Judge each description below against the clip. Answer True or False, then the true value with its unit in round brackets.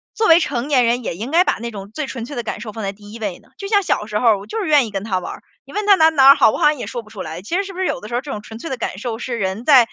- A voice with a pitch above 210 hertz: True (235 Hz)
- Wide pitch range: True (6.0 semitones)